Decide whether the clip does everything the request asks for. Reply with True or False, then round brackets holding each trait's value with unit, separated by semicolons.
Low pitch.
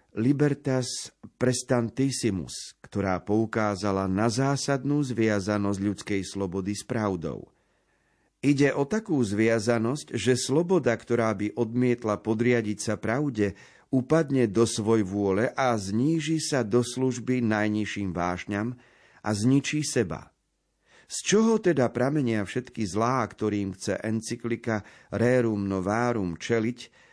True (115 Hz)